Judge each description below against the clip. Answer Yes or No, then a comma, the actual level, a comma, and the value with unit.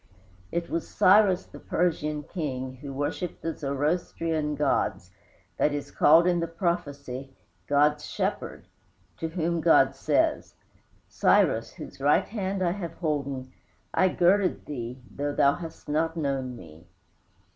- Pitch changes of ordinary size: Yes, average, 3.7 semitones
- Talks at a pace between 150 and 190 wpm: No, slow, 135 wpm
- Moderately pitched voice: Yes, medium, 150 Hz